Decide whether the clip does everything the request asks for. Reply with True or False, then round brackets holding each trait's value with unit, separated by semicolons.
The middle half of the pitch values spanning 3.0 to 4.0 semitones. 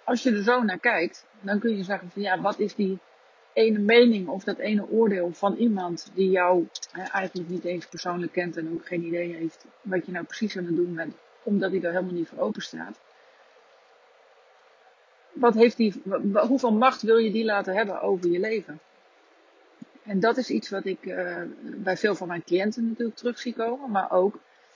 False (4.4 semitones)